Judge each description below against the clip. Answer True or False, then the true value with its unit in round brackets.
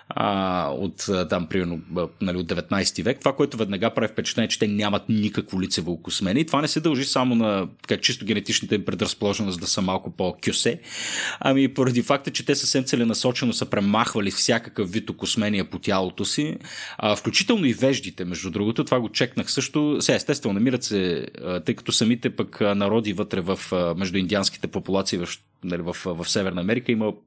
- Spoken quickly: True (170 wpm)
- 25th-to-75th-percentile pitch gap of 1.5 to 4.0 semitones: False (5.2 semitones)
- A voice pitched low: True (105 Hz)